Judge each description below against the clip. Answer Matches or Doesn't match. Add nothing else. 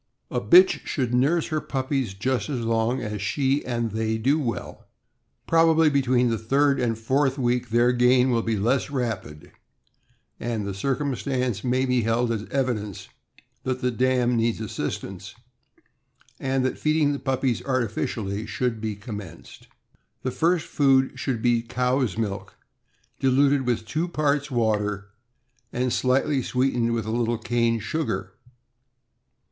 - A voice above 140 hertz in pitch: Doesn't match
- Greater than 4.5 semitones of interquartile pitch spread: Doesn't match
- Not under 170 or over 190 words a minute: Doesn't match